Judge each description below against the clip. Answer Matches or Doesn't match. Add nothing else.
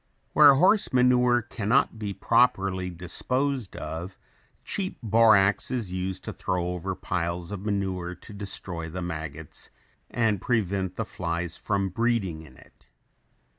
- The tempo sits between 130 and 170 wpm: Matches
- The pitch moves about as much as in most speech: Matches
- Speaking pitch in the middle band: Doesn't match